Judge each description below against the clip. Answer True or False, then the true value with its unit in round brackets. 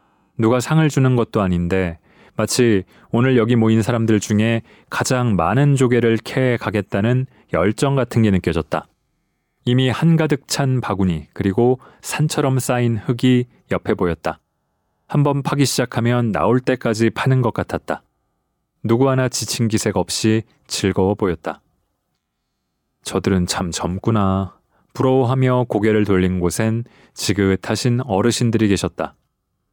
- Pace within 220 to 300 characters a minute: True (270 characters per minute)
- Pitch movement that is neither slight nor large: True (4.7 semitones)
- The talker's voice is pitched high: False (115 Hz)